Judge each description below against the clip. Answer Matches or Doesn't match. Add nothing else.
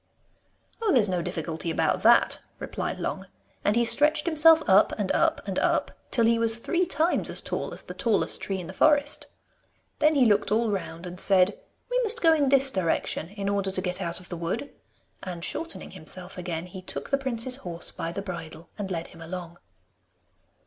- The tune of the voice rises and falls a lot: Matches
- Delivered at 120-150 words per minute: Doesn't match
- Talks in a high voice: Matches